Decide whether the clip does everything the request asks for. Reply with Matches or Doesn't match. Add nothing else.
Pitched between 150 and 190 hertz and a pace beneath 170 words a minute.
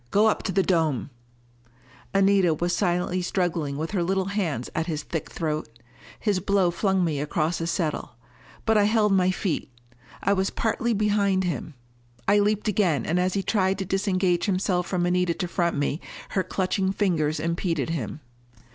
Doesn't match